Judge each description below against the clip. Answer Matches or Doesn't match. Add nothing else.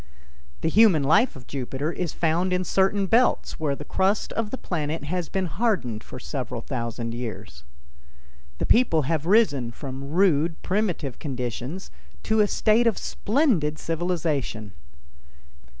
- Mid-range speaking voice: Matches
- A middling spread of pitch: Doesn't match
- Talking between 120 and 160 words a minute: Matches